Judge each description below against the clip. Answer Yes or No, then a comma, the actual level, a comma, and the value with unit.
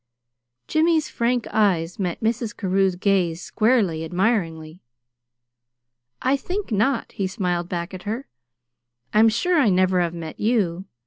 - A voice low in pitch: No, high, 195 Hz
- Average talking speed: No, slow, 130 wpm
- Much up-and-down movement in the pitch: No, average, 4.9 semitones